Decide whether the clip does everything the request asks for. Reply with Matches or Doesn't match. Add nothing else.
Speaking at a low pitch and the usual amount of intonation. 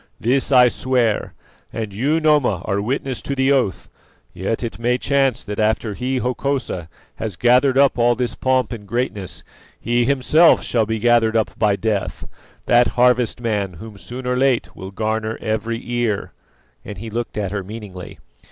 Matches